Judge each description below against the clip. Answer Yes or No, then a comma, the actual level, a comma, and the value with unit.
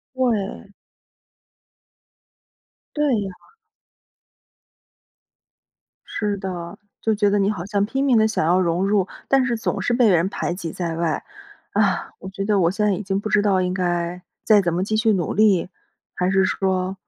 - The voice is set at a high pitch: Yes, high, 195 Hz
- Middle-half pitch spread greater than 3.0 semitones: No, average, 2.7 semitones